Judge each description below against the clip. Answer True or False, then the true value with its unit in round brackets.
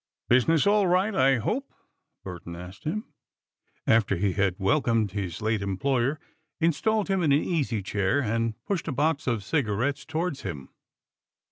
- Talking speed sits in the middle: True (150 wpm)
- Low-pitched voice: True (125 Hz)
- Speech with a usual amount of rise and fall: False (8.2 semitones)